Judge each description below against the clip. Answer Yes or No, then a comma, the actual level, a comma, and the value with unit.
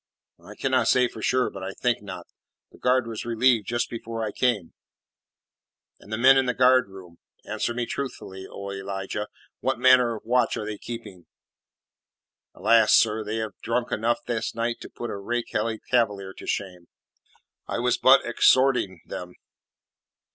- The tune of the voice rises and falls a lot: No, average, 3.6 semitones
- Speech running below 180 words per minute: Yes, average, 160 wpm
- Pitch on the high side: No, low, 115 Hz